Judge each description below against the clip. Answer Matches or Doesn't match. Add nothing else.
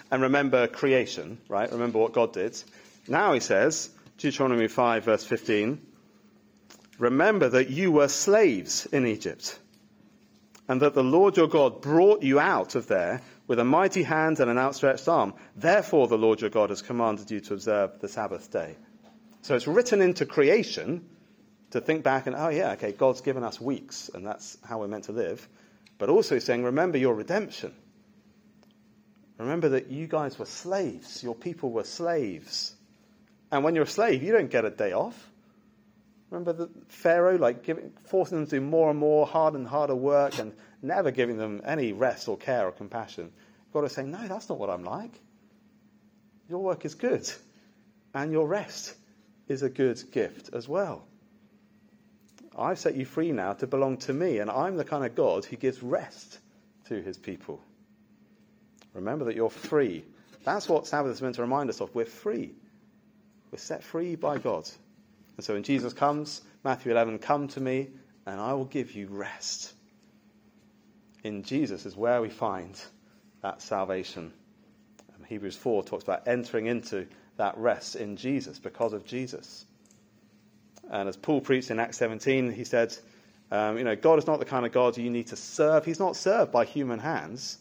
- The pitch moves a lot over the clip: Matches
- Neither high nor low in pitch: Matches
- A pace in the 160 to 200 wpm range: Matches